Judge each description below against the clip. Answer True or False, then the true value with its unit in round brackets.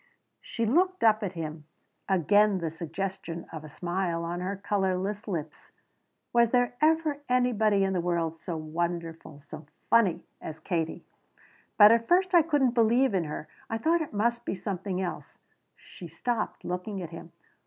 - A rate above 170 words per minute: False (165 wpm)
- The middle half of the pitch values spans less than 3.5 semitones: False (5.6 semitones)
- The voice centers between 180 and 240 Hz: True (190 Hz)